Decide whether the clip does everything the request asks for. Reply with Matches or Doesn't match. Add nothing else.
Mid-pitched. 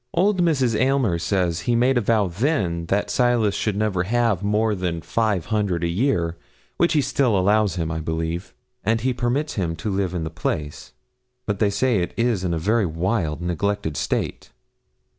Doesn't match